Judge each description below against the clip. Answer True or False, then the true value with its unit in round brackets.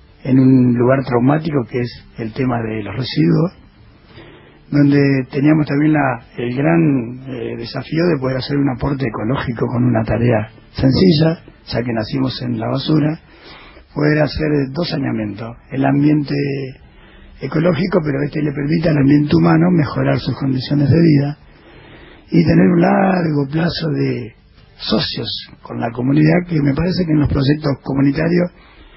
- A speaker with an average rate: True (150 wpm)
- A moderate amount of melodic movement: True (3.3 semitones)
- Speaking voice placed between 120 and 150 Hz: True (140 Hz)